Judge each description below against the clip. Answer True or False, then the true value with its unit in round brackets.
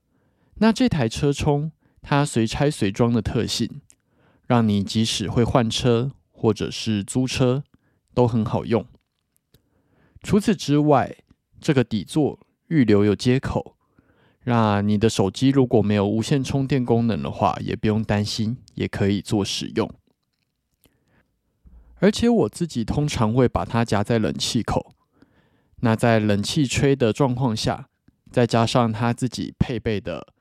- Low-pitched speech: True (115 Hz)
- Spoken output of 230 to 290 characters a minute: False (205 characters per minute)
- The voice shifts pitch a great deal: False (4.0 semitones)